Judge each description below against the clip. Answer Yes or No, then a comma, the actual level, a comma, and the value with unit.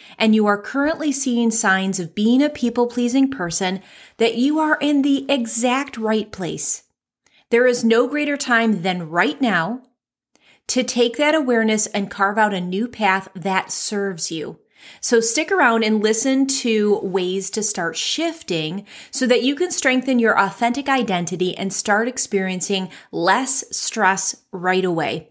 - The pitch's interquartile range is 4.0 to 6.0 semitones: Yes, average, 4.9 semitones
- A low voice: No, high, 225 Hz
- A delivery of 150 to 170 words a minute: Yes, average, 155 wpm